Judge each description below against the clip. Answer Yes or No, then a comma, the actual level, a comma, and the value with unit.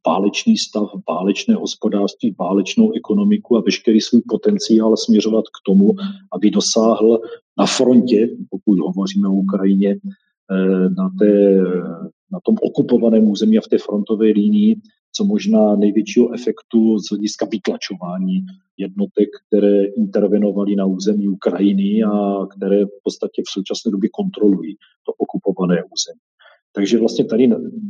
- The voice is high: No, low, 110 Hz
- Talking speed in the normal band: Yes, average, 125 wpm